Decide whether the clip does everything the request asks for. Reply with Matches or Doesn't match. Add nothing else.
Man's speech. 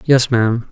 Matches